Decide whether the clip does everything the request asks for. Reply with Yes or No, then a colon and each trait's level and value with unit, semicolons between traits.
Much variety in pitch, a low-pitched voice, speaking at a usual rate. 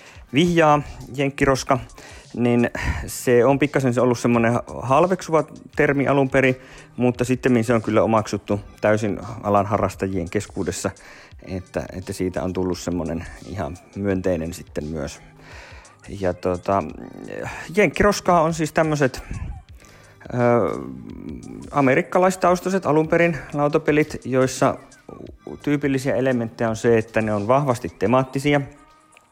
Yes: wide, 6.8 semitones; low, 120 Hz; average, 105 wpm